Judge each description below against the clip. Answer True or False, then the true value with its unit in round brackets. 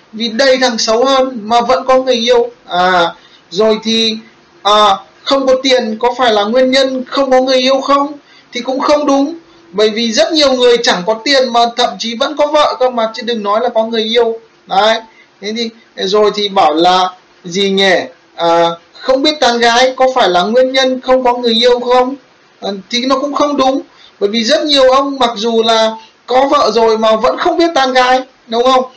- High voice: True (245 Hz)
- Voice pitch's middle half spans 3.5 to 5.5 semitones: False (3.0 semitones)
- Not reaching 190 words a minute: False (215 wpm)